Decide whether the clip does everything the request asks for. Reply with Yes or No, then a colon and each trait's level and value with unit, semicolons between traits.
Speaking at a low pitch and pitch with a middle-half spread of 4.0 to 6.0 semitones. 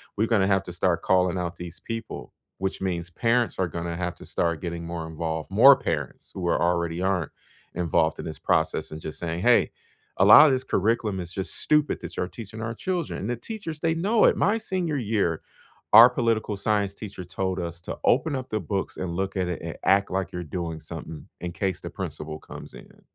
Yes: very low, 95 Hz; average, 5.0 semitones